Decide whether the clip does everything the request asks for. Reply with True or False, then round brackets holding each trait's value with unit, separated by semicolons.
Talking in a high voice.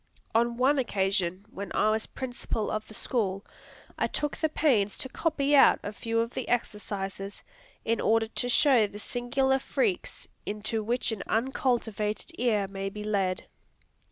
True (225 Hz)